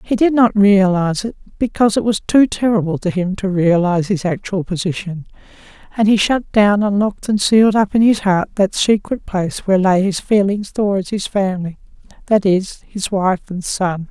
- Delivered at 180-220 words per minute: Yes, average, 195 wpm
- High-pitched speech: Yes, high, 195 Hz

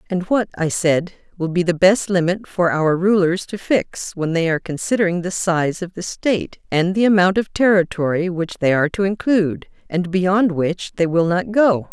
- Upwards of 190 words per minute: Yes, average, 200 wpm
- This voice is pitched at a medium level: Yes, medium, 180 Hz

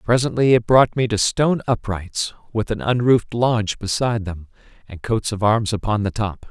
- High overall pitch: No, low, 110 Hz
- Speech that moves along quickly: No, average, 185 wpm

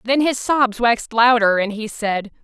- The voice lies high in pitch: Yes, high, 230 Hz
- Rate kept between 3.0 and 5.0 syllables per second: Yes, 4.5 syllables/s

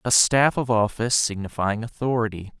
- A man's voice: Yes, male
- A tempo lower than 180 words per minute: Yes, average, 140 wpm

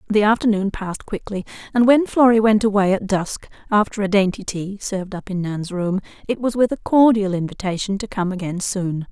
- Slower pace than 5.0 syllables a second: No, 5.4 syllables/s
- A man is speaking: No, female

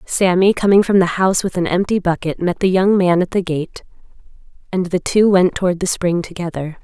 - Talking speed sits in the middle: No, fast, 210 wpm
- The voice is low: No, medium, 180 Hz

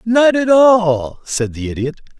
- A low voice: No, medium, 185 Hz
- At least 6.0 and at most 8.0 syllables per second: No, 3.8 syllables/s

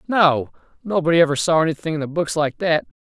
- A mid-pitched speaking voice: Yes, medium, 155 Hz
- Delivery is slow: No, average, 200 wpm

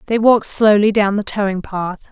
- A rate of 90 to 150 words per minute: No, average, 200 wpm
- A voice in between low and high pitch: No, high, 205 Hz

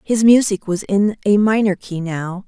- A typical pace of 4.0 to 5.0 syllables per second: Yes, 4.4 syllables/s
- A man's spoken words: No, female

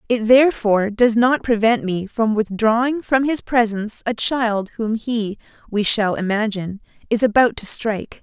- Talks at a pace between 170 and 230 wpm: No, average, 160 wpm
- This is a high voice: Yes, high, 225 Hz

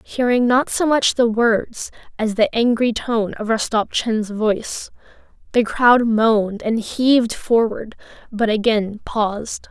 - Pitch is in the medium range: No, high, 225 Hz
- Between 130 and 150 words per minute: Yes, slow, 135 wpm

